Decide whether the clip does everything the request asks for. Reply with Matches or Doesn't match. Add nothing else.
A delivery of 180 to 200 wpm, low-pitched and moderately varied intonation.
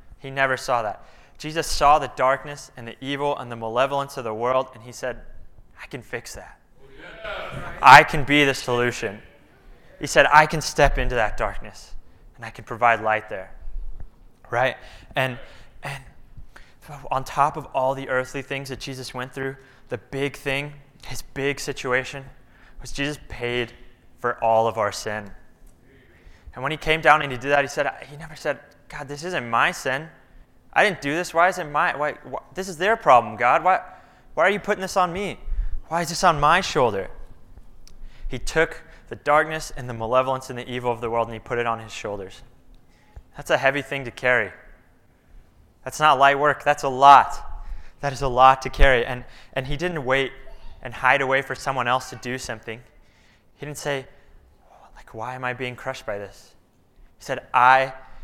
Matches